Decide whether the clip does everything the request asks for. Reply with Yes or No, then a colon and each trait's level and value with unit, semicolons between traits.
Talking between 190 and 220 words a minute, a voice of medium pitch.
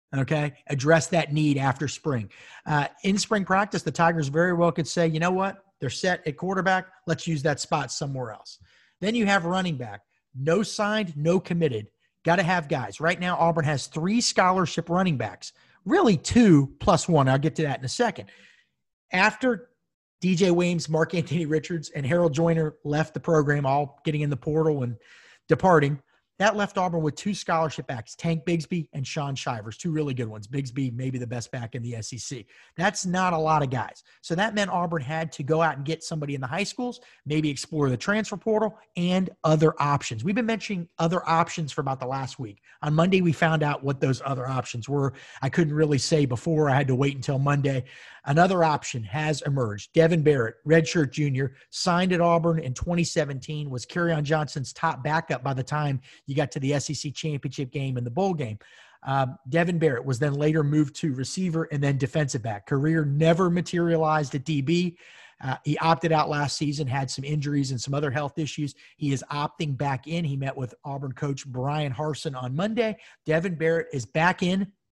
Yes: average, 195 wpm; medium, 155 Hz